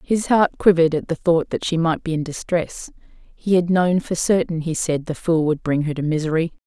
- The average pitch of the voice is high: No, medium, 165 Hz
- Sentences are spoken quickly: Yes, fast, 235 wpm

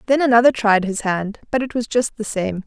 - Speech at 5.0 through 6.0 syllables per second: Yes, 5.5 syllables/s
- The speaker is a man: No, female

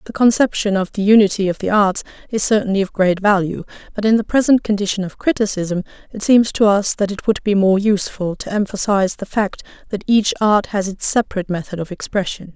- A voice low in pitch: No, high, 200 Hz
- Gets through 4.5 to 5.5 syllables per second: No, 5.9 syllables/s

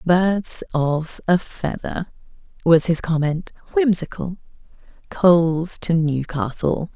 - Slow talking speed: Yes, slow, 95 wpm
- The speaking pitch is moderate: Yes, medium, 170 Hz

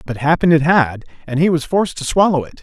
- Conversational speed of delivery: No, fast, 250 wpm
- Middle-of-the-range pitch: Yes, medium, 150 Hz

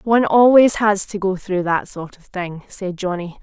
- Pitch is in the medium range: No, high, 195 Hz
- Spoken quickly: Yes, fast, 210 wpm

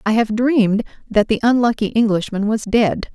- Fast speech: No, average, 170 wpm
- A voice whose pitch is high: Yes, high, 220 Hz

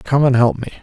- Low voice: Yes, low, 125 Hz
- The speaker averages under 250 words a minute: No, fast, 290 wpm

